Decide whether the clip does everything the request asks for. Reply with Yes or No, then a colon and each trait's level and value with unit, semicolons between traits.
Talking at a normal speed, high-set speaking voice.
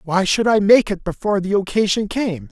No: fast, 215 wpm; high, 195 Hz